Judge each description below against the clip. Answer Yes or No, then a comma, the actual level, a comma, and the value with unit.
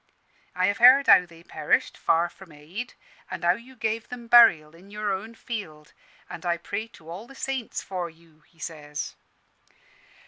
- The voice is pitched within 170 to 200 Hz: Yes, medium, 185 Hz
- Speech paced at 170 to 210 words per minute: Yes, average, 175 wpm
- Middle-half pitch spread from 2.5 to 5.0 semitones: No, wide, 5.6 semitones